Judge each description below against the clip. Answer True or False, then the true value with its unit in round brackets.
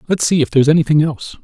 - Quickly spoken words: True (250 wpm)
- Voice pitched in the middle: True (150 Hz)